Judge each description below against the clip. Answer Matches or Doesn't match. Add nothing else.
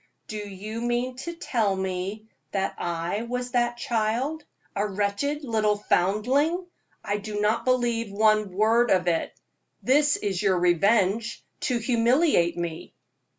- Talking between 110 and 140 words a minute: Matches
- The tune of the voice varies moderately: Matches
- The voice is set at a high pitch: Matches